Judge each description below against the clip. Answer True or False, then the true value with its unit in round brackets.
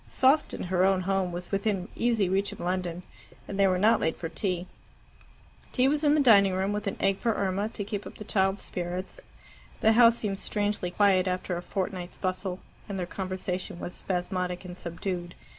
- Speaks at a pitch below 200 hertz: True (190 Hz)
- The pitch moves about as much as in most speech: False (2.2 semitones)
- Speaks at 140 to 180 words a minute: False (190 wpm)